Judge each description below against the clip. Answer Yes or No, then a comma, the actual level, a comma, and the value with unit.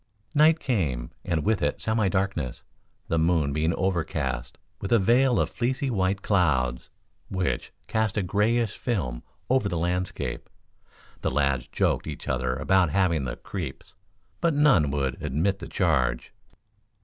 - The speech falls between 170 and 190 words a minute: No, average, 145 wpm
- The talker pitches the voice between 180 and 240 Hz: No, very low, 90 Hz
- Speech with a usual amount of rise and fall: No, wide, 7.0 semitones